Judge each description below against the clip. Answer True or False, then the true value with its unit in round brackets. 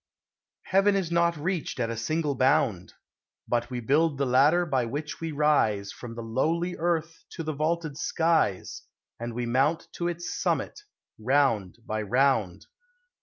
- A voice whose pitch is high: False (145 Hz)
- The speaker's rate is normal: True (155 wpm)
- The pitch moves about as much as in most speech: False (5.7 semitones)